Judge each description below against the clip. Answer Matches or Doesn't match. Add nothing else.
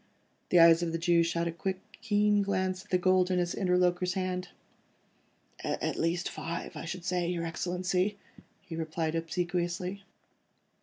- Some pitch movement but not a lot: Doesn't match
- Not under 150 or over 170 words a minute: Matches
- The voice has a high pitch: Doesn't match